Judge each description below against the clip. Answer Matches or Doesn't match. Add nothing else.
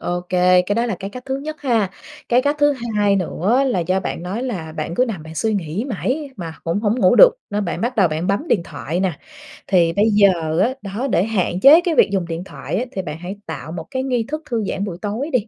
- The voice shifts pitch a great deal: Matches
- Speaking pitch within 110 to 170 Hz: Doesn't match